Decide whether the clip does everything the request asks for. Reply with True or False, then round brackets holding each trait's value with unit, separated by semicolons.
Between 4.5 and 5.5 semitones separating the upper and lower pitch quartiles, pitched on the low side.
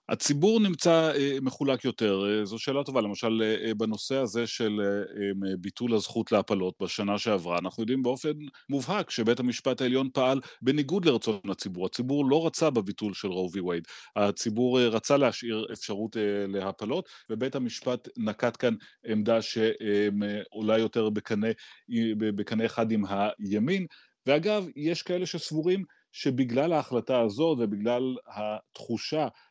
True (4.9 semitones; 115 Hz)